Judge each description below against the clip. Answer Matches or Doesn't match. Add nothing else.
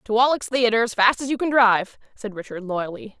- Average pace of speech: Doesn't match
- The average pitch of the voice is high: Matches